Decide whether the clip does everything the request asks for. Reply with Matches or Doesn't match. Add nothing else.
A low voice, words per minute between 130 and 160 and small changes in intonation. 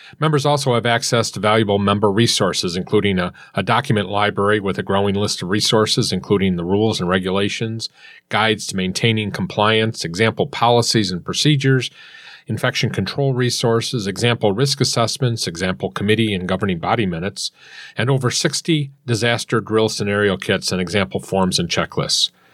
Doesn't match